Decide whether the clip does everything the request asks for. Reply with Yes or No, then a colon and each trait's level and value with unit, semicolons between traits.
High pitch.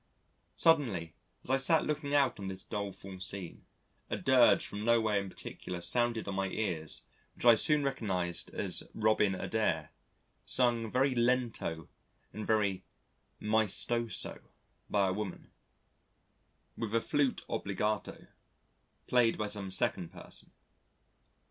No: low, 110 Hz